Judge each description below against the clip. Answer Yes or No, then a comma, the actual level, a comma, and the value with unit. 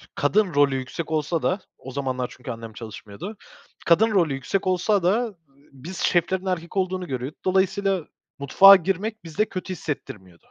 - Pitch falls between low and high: Yes, medium, 170 Hz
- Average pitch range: No, wide, 6.0 semitones